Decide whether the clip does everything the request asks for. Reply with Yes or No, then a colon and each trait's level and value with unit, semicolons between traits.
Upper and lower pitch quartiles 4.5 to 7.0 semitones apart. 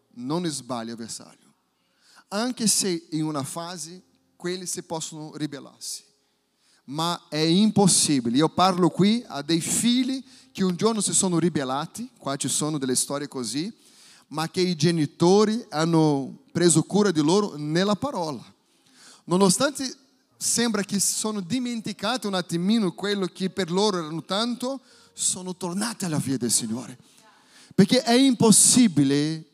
Yes: wide, 5.6 semitones